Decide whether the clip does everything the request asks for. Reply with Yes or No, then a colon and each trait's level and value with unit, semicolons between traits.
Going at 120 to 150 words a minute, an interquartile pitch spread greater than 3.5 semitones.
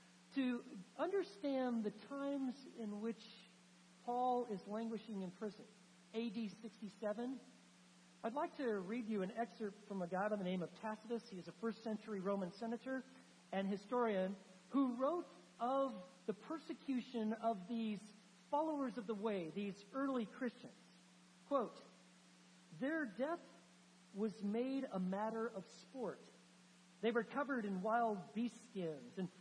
Yes: average, 140 wpm; average, 4.3 semitones